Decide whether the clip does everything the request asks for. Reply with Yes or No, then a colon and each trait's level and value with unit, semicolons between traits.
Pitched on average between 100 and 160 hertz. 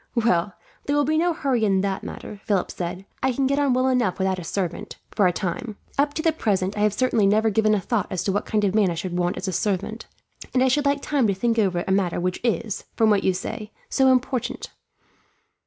No: high, 210 Hz